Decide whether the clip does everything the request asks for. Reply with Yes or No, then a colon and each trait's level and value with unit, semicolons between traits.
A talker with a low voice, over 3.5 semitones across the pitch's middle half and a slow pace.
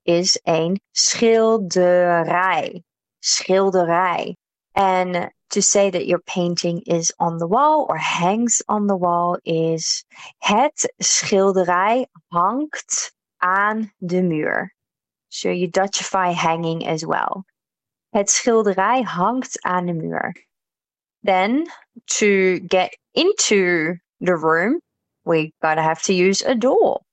No: medium, 185 Hz; average, 4.0 semitones; slow, 115 wpm